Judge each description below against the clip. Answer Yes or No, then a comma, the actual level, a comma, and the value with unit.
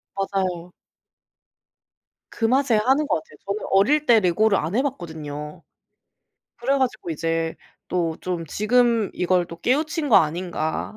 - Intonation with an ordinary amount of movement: No, wide, 6.7 semitones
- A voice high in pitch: Yes, high, 195 Hz